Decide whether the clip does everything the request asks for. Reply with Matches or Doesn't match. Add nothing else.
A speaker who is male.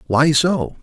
Matches